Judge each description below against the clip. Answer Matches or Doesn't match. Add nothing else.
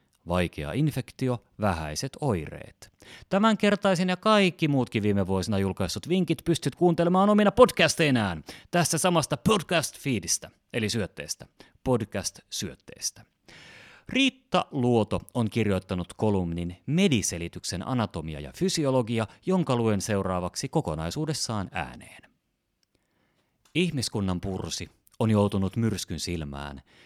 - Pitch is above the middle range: Doesn't match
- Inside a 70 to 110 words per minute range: Matches